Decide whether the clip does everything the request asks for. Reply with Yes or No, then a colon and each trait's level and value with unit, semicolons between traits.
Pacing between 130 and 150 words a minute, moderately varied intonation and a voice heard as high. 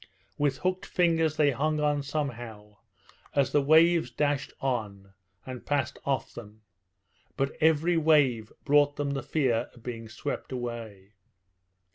No: slow, 135 wpm; average, 4.2 semitones; medium, 140 Hz